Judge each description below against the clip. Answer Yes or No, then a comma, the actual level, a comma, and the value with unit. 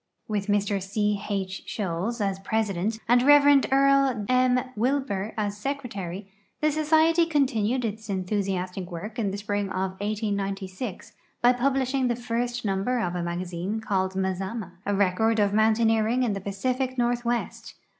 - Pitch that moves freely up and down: No, average, 4.2 semitones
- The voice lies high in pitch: Yes, high, 215 Hz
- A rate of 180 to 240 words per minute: No, average, 145 wpm